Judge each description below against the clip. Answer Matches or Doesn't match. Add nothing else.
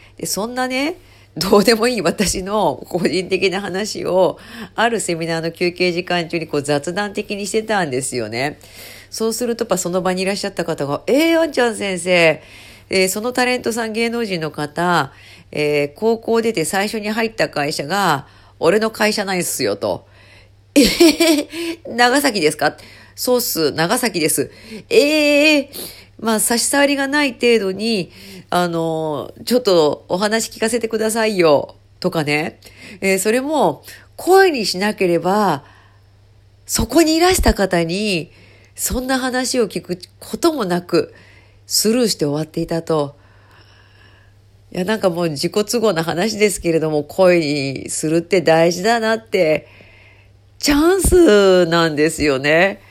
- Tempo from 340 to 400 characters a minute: Doesn't match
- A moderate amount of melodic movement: Doesn't match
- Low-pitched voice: Doesn't match